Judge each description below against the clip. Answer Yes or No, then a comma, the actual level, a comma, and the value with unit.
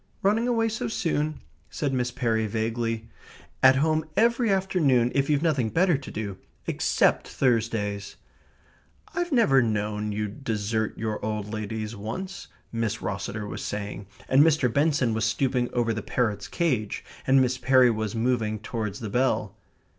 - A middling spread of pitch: Yes, average, 5.0 semitones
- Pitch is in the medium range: No, low, 120 Hz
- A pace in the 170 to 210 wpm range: No, average, 150 wpm